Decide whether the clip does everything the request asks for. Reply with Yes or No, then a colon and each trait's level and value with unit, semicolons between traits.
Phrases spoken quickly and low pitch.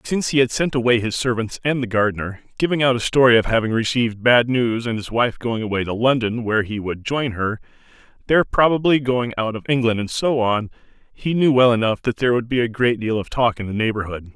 Yes: fast, 235 wpm; low, 120 Hz